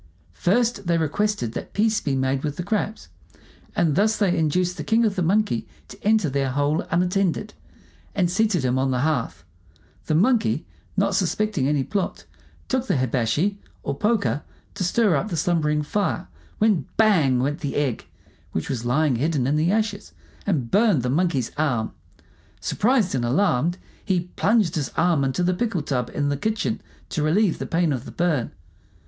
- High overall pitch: No, medium, 170 Hz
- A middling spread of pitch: No, wide, 6.5 semitones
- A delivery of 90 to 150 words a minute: No, average, 175 wpm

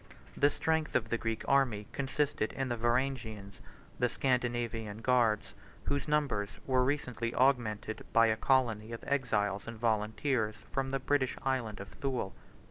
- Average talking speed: Yes, average, 145 wpm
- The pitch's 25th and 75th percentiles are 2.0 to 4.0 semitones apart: Yes, average, 3.5 semitones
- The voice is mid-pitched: No, low, 120 Hz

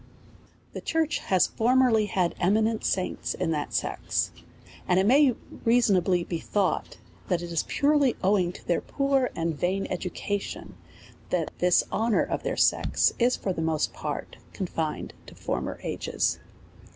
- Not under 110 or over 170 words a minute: Yes, average, 150 wpm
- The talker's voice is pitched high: Yes, high, 195 Hz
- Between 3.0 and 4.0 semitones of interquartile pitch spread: No, average, 5.2 semitones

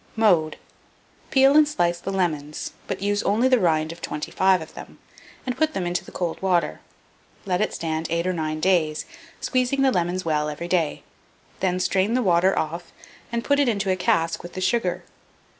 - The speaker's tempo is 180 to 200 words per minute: Yes, average, 190 wpm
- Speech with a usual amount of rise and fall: Yes, average, 4.2 semitones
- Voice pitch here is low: No, medium, 180 Hz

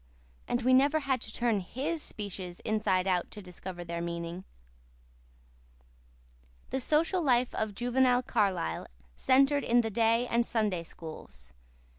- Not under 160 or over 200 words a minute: No, slow, 135 wpm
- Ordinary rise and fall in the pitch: No, wide, 5.9 semitones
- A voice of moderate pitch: No, high, 225 Hz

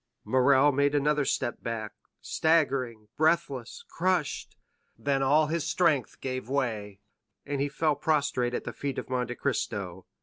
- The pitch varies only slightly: No, average, 3.5 semitones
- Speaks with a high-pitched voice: No, medium, 140 Hz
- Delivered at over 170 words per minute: No, average, 140 wpm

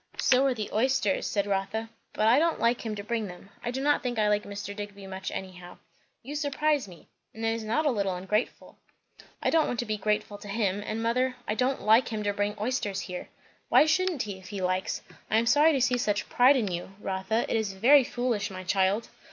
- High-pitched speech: Yes, high, 215 Hz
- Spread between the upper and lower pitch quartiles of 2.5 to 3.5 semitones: No, average, 4.0 semitones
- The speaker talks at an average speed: No, fast, 230 wpm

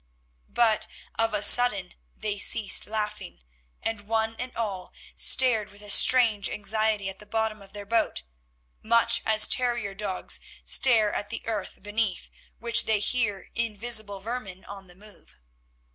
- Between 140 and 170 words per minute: Yes, average, 145 wpm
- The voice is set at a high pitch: Yes, high, 215 Hz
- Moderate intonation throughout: No, narrow, 2.0 semitones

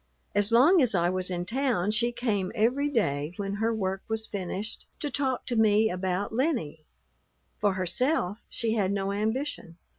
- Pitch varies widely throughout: No, average, 4.3 semitones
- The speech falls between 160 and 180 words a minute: Yes, average, 170 wpm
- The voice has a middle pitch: No, high, 210 Hz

